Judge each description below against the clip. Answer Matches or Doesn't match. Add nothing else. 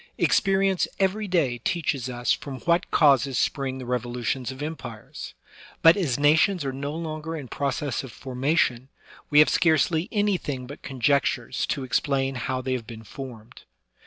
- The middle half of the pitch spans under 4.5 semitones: Matches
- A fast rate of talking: Doesn't match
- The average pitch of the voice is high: Doesn't match